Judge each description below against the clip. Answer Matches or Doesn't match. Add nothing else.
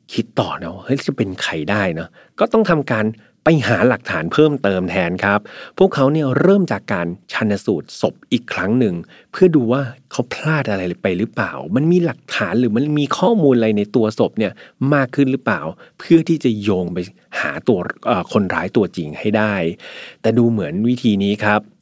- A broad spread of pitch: Matches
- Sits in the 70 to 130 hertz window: Matches